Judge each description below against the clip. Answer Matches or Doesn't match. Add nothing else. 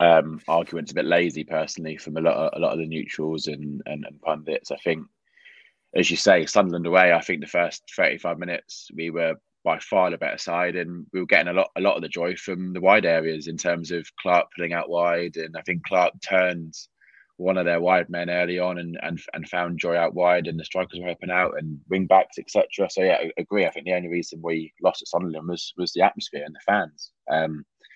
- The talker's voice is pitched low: Matches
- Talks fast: Matches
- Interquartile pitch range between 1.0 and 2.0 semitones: Matches